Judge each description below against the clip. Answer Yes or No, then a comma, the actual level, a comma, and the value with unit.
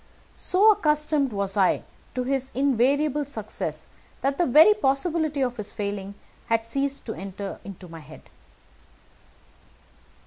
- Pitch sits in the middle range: No, very high, 265 Hz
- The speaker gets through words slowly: Yes, slow, 130 wpm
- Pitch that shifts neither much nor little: No, wide, 6.4 semitones